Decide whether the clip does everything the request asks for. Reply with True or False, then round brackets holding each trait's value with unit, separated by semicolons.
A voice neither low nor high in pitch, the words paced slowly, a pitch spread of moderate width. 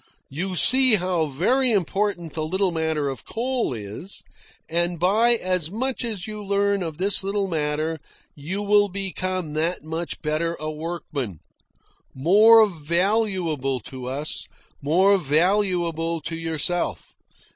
True (175 Hz; 130 wpm; 4.4 semitones)